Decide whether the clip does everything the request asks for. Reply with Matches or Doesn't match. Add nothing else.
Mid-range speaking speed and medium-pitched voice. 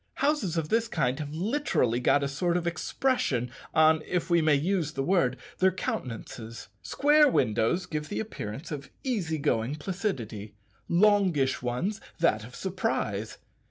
Matches